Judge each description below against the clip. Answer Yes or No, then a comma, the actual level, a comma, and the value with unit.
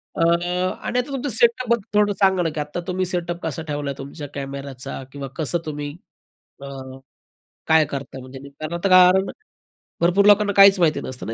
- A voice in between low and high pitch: Yes, medium, 170 Hz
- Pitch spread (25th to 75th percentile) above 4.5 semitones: Yes, average, 5.1 semitones